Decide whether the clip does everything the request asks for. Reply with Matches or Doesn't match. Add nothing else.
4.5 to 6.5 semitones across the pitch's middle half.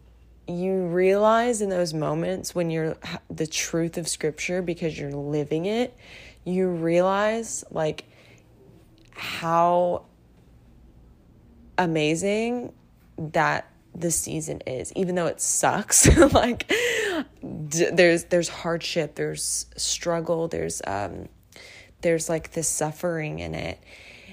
Matches